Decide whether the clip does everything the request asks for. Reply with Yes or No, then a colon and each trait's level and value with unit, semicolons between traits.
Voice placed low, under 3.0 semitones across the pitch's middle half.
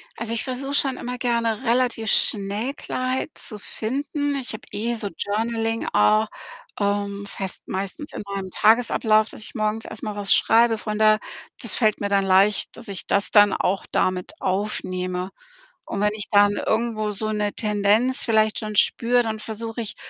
No: high, 215 Hz; narrow, 2.4 semitones